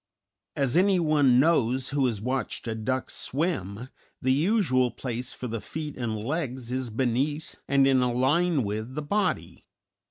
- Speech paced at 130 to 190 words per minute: Yes, average, 155 wpm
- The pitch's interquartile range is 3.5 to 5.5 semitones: Yes, average, 3.8 semitones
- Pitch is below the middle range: Yes, low, 130 Hz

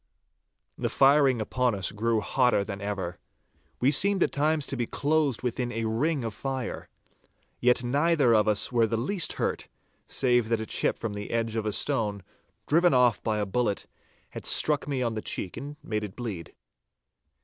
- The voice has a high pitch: No, low, 120 Hz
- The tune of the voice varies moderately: Yes, average, 4.3 semitones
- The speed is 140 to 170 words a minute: No, average, 180 wpm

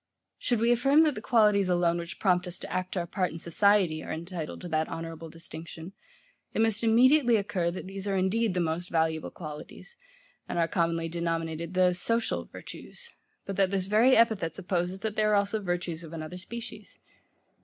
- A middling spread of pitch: Yes, average, 4.2 semitones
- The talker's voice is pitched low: No, medium, 185 Hz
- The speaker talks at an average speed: Yes, average, 185 wpm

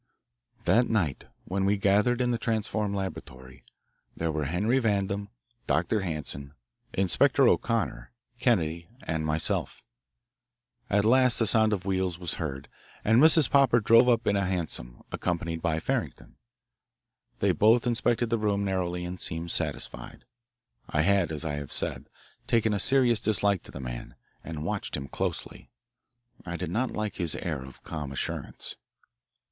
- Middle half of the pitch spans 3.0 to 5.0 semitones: No, wide, 5.6 semitones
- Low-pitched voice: Yes, very low, 95 Hz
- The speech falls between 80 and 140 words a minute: No, average, 150 wpm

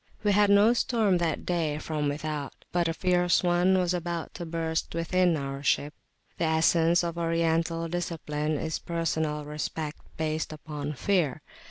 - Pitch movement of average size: No, narrow, 2.3 semitones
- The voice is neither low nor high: Yes, medium, 165 Hz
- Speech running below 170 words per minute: Yes, average, 155 wpm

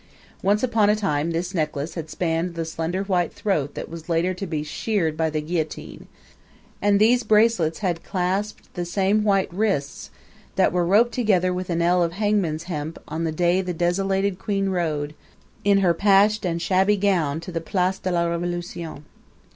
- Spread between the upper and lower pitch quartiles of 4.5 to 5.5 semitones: No, average, 3.2 semitones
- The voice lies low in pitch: No, medium, 180 Hz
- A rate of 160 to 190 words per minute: Yes, average, 180 wpm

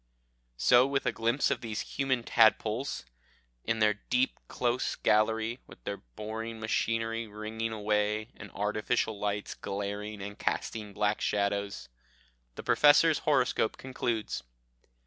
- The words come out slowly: Yes, slow, 125 wpm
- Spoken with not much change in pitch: Yes, narrow, 2.1 semitones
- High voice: No, low, 110 Hz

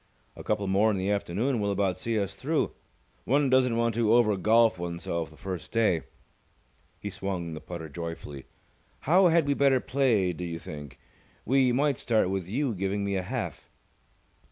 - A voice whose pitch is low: Yes, low, 100 Hz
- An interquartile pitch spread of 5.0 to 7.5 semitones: Yes, average, 5.3 semitones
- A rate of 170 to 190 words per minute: Yes, average, 180 wpm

